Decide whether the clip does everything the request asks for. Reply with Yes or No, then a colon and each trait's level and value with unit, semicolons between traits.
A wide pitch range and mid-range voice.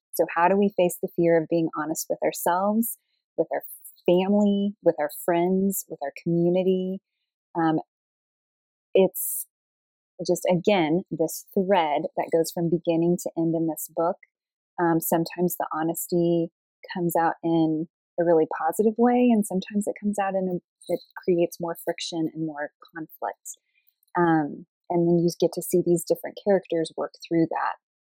No: narrow, 2.4 semitones; medium, 175 Hz